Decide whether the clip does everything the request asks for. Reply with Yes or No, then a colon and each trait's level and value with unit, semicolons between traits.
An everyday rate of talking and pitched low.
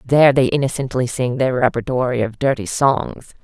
Yes: average, 155 wpm; low, 125 Hz